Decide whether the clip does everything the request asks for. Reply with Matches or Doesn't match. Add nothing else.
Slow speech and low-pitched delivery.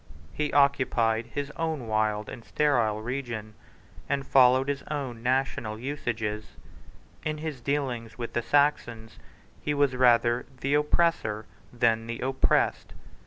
Matches